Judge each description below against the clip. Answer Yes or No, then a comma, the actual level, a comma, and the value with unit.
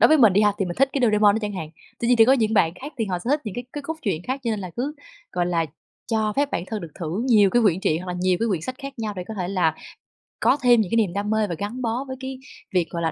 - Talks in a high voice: Yes, high, 215 Hz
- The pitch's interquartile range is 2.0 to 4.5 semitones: No, average, 5.2 semitones